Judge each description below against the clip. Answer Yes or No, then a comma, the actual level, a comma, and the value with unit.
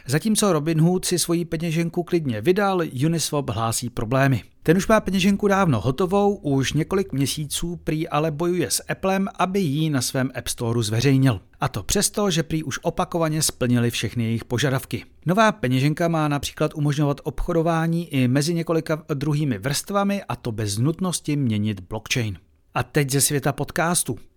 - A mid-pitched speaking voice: Yes, medium, 150 Hz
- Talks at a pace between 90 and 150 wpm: No, average, 160 wpm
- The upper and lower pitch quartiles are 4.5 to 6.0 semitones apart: Yes, average, 5.3 semitones